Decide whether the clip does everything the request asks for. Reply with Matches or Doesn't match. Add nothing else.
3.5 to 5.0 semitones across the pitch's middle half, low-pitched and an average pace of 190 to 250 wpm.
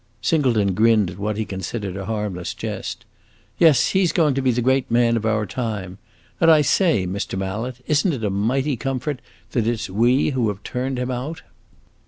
Matches